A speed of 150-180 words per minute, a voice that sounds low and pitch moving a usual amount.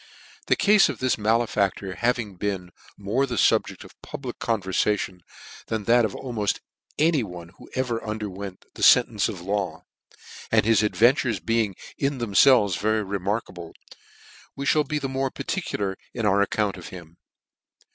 Yes: average, 155 wpm; low, 105 Hz; average, 4.0 semitones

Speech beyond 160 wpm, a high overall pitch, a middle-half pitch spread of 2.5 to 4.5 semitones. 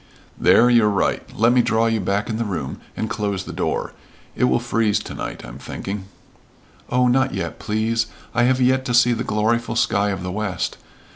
No: average, 200 wpm; low, 110 Hz; average, 3.3 semitones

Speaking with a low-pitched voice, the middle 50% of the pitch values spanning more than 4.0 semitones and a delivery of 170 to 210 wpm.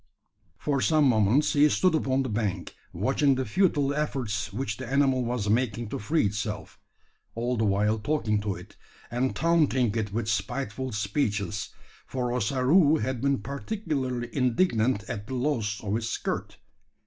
No: low, 125 Hz; average, 4.6 semitones; average, 155 wpm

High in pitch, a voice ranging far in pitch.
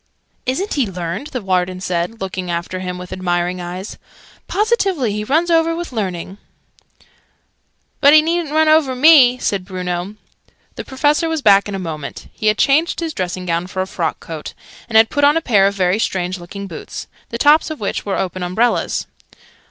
Yes: high, 200 Hz; wide, 8.1 semitones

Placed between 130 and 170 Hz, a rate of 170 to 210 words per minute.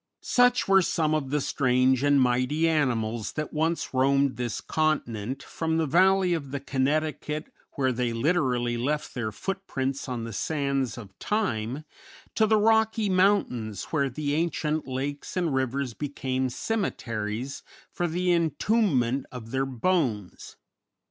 No: medium, 140 Hz; average, 140 wpm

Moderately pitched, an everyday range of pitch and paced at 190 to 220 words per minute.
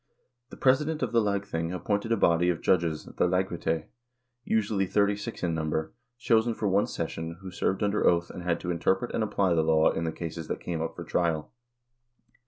No: very low, 90 Hz; average, 3.8 semitones; average, 195 wpm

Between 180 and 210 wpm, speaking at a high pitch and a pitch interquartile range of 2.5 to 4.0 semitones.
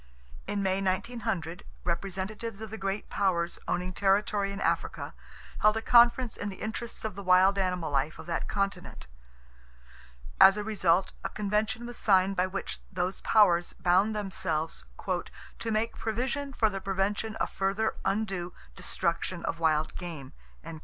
No: average, 150 wpm; high, 195 Hz; average, 2.9 semitones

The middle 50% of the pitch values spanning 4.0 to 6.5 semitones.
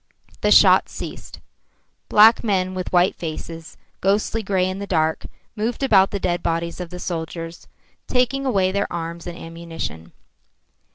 No: average, 3.2 semitones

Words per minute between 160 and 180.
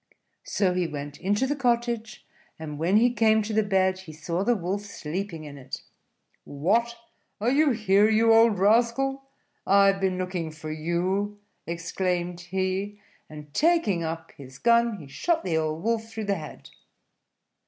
Yes: average, 165 wpm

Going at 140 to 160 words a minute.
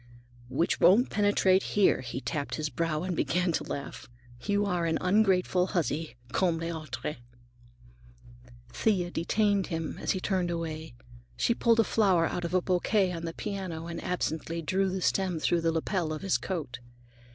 No: average, 170 wpm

